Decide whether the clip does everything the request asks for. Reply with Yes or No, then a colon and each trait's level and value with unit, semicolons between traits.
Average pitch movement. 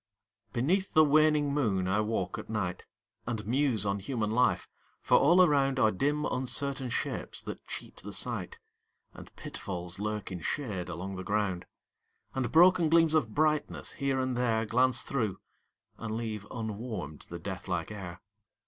No: wide, 5.8 semitones